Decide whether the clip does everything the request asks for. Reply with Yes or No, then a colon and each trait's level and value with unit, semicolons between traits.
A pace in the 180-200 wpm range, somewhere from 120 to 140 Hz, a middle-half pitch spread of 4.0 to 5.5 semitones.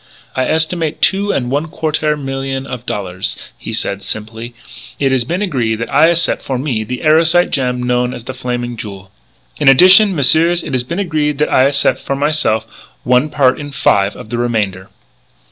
Yes: average, 185 wpm; low, 135 Hz; average, 4.3 semitones